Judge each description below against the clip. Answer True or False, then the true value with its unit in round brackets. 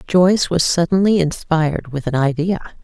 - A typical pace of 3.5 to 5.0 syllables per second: False (5.2 syllables/s)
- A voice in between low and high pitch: True (165 Hz)